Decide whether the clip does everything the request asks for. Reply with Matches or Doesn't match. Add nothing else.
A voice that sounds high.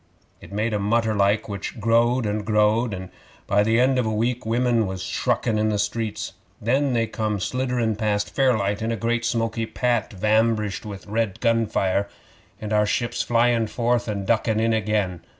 Doesn't match